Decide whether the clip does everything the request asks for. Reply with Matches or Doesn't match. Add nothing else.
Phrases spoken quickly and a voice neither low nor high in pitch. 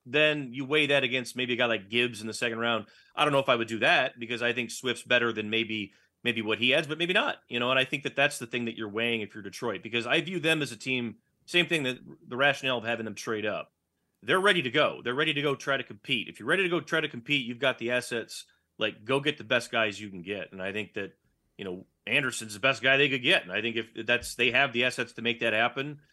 Doesn't match